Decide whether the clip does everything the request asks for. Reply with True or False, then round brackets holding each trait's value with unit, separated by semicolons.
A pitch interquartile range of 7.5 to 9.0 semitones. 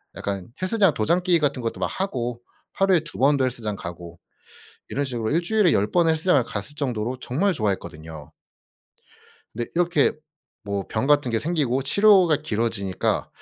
True (7.8 semitones)